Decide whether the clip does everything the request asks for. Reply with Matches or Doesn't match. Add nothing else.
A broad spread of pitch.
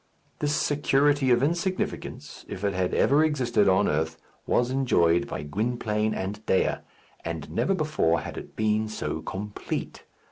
Matches